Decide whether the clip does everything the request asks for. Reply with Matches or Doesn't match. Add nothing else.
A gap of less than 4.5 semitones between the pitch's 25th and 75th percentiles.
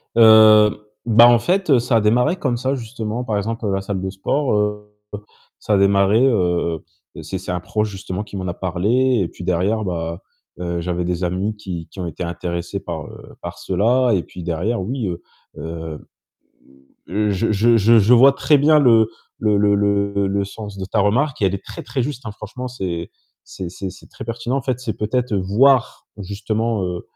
Matches